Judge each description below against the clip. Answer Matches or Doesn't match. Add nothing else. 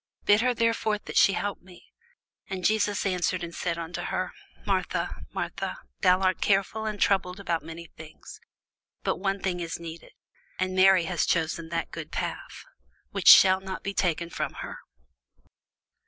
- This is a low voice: Doesn't match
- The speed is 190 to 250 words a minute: Doesn't match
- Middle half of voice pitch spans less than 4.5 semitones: Matches